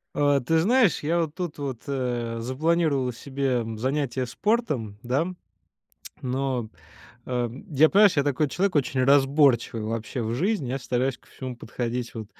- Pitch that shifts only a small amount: No, average, 3.7 semitones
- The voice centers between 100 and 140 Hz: Yes, low, 135 Hz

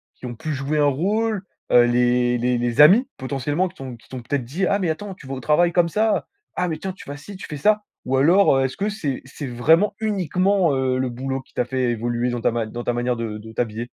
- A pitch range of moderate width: No, wide, 6.8 semitones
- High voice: No, low, 135 Hz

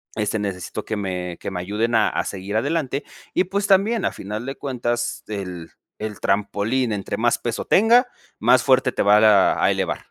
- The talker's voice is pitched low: Yes, low, 110 Hz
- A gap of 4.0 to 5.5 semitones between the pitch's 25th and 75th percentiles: Yes, average, 4.5 semitones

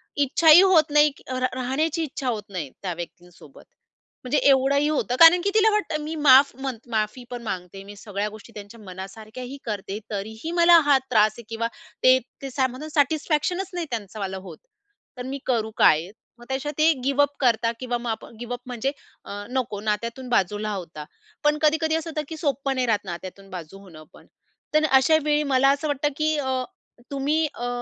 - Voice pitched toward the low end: No, very high, 255 Hz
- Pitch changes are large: Yes, wide, 5.7 semitones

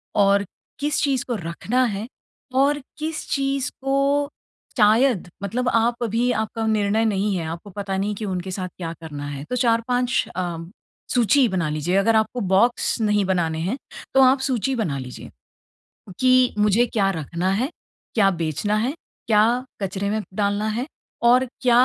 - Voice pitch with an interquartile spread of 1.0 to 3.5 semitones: No, average, 4.5 semitones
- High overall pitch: Yes, high, 215 Hz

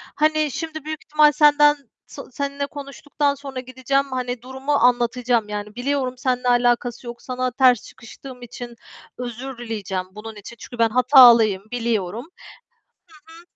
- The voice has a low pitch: No, very high, 250 Hz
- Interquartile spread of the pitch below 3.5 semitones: Yes, average, 2.9 semitones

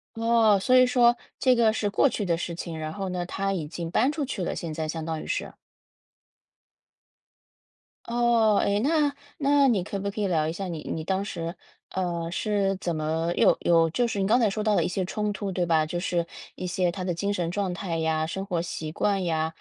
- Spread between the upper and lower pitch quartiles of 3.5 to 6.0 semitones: Yes, average, 4.2 semitones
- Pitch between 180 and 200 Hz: Yes, high, 190 Hz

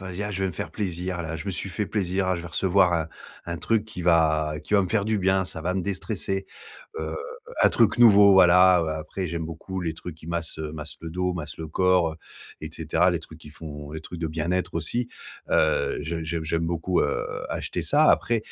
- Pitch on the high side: No, very low, 85 Hz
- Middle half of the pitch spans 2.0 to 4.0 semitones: Yes, average, 2.9 semitones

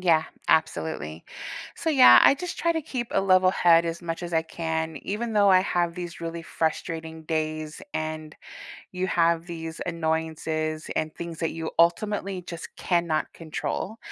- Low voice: No, medium, 165 Hz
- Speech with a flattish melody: Yes, narrow, 2.3 semitones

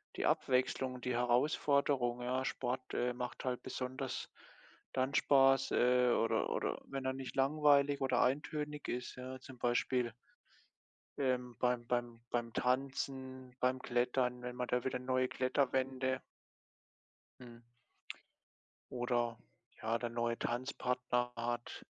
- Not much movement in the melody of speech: Yes, narrow, 1.4 semitones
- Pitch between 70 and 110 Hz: No, low, 125 Hz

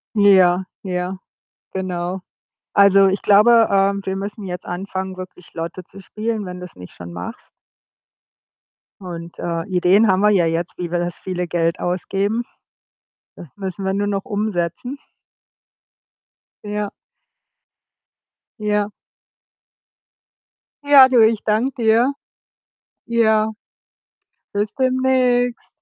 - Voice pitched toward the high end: Yes, high, 195 Hz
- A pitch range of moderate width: Yes, average, 3.2 semitones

